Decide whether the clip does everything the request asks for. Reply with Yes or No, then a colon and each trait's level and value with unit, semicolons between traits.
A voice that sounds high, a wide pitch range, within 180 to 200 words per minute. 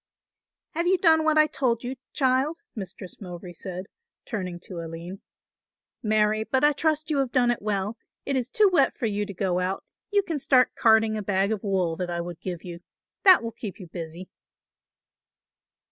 Yes: high, 215 Hz; wide, 6.6 semitones; average, 190 wpm